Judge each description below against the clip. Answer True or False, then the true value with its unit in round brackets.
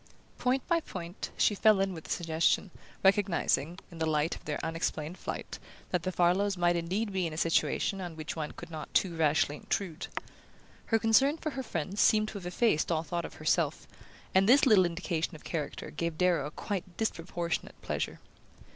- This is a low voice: False (175 Hz)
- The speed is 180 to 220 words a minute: True (190 wpm)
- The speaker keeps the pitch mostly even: False (3.6 semitones)